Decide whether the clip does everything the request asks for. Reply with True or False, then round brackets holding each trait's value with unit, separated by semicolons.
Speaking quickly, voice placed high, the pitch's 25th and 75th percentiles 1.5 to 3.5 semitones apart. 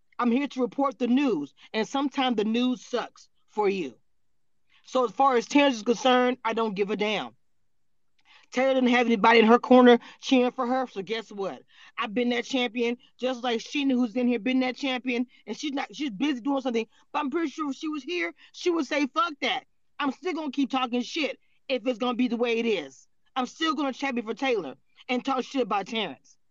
True (220 wpm; 255 Hz; 2.5 semitones)